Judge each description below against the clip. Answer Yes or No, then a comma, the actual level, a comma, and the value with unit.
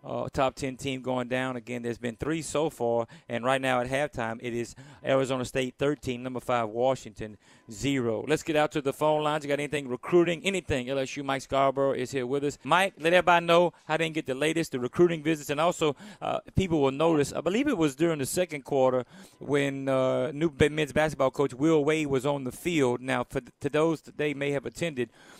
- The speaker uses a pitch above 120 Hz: Yes, medium, 140 Hz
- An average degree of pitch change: Yes, average, 3.3 semitones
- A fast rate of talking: Yes, fast, 220 wpm